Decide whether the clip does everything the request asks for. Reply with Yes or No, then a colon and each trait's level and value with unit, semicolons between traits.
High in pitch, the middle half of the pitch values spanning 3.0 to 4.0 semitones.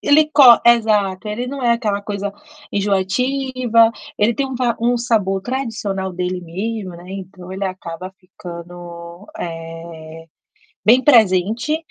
No: high, 200 Hz; average, 4.6 semitones